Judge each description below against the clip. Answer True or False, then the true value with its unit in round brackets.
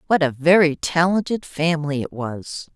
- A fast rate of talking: False (155 wpm)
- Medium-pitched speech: True (155 Hz)